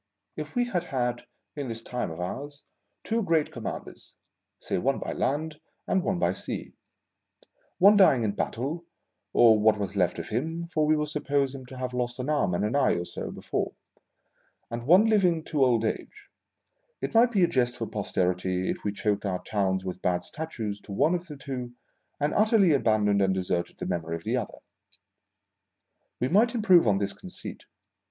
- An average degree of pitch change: No, wide, 7.8 semitones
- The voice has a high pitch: No, low, 125 Hz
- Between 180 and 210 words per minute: Yes, average, 190 wpm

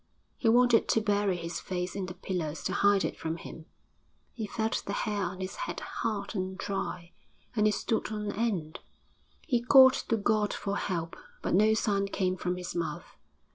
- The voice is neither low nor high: No, high, 200 Hz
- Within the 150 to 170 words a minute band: No, average, 185 wpm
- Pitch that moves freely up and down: No, average, 3.2 semitones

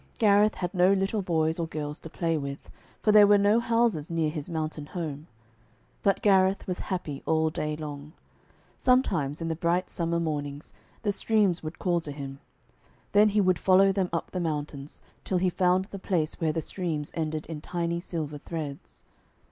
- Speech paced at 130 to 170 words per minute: No, average, 180 wpm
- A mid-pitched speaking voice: Yes, medium, 170 Hz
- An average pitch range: Yes, average, 3.7 semitones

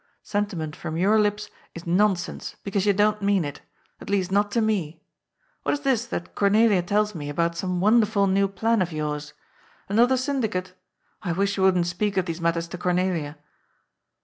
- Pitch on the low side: No, high, 195 Hz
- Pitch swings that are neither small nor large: Yes, average, 3.5 semitones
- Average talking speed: Yes, average, 180 wpm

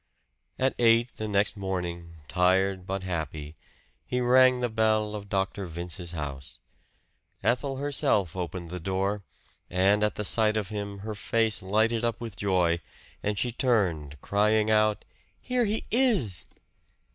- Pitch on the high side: No, low, 100 Hz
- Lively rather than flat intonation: No, average, 3.8 semitones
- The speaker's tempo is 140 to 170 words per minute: Yes, average, 145 wpm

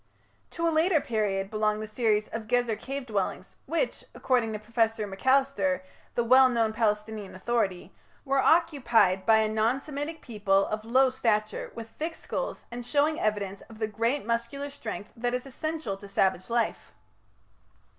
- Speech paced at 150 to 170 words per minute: Yes, average, 160 wpm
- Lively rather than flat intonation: No, average, 3.9 semitones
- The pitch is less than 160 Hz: No, high, 230 Hz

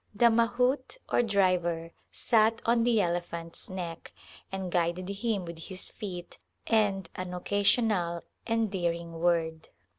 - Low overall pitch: No, medium, 185 Hz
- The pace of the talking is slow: Yes, slow, 120 wpm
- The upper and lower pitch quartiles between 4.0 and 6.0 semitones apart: Yes, average, 4.5 semitones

